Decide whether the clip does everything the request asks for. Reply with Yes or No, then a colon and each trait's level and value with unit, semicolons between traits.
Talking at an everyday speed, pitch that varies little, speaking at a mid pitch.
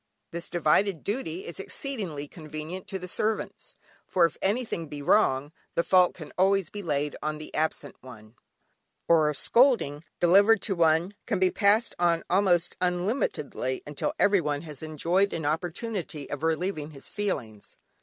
No: average, 155 wpm; average, 4.4 semitones; medium, 170 Hz